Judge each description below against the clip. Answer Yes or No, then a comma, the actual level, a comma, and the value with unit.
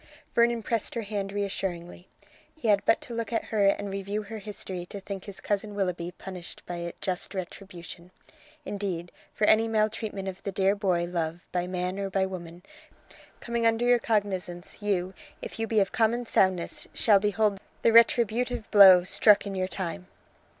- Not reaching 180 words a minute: Yes, average, 170 wpm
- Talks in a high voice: Yes, high, 200 Hz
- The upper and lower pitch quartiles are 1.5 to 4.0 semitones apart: Yes, average, 2.9 semitones